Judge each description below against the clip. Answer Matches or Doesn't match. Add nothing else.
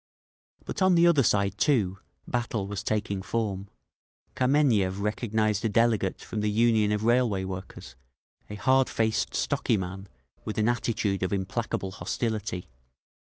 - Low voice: Matches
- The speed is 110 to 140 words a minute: Matches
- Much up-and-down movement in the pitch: Doesn't match